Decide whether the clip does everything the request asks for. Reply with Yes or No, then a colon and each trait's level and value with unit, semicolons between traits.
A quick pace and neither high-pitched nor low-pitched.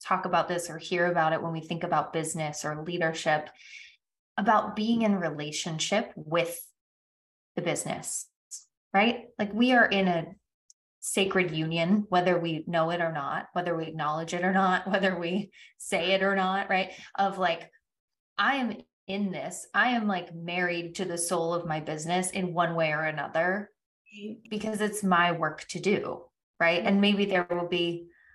No: average, 170 wpm; medium, 175 Hz